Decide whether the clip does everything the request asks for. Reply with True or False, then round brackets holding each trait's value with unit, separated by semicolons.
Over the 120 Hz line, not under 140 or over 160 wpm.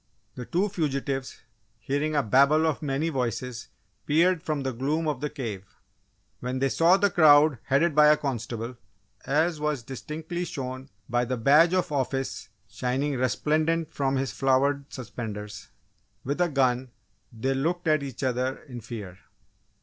True (140 Hz; 150 wpm)